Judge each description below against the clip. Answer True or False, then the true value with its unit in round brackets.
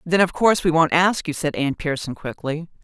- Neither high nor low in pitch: True (160 Hz)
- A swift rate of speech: True (235 wpm)